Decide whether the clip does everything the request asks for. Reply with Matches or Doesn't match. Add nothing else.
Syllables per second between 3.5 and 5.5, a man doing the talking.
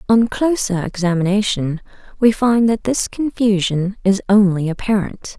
Doesn't match